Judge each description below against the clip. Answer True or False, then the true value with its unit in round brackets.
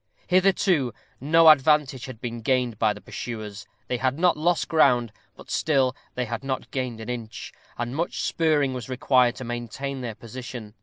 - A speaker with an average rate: True (170 wpm)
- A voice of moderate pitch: False (130 Hz)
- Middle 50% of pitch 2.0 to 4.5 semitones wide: True (3.3 semitones)